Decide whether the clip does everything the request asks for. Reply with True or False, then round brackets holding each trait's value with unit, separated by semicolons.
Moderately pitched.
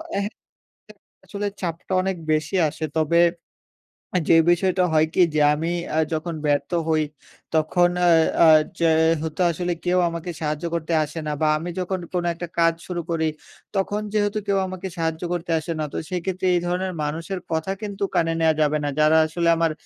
True (170 Hz)